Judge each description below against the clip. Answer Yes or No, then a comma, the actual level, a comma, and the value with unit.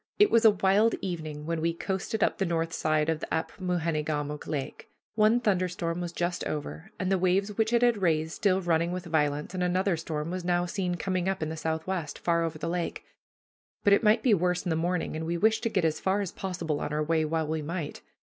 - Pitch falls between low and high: Yes, medium, 175 Hz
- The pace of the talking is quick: Yes, fast, 235 wpm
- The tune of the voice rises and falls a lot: No, average, 3.0 semitones